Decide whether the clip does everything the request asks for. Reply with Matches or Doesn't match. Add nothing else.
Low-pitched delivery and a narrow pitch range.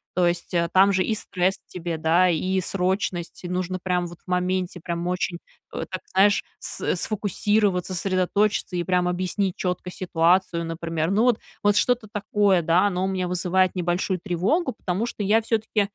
Doesn't match